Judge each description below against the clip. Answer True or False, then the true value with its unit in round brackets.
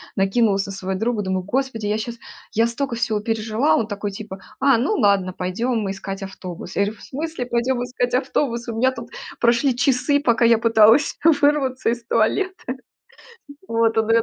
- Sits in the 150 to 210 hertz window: False (230 Hz)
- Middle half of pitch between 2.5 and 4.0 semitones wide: True (3.6 semitones)